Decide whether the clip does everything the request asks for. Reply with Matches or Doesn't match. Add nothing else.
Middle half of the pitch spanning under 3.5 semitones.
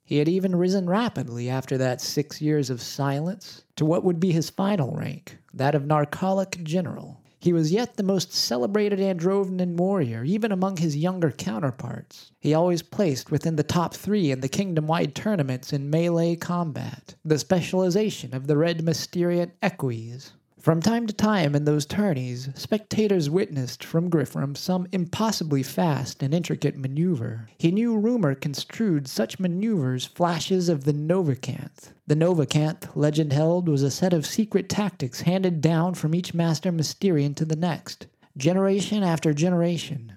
Doesn't match